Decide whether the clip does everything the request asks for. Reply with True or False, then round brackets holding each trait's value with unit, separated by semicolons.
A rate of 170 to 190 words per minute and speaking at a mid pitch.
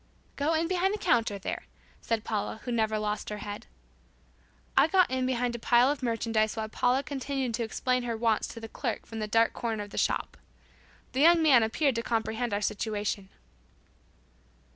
False (185 wpm; 230 Hz)